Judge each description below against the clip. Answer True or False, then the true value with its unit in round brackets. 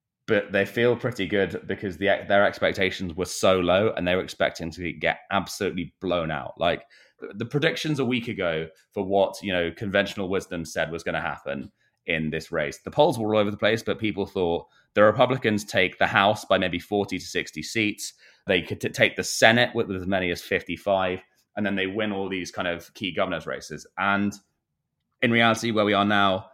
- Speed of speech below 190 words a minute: False (205 wpm)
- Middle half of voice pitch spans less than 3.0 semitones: True (2.4 semitones)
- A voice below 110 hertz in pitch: True (100 Hz)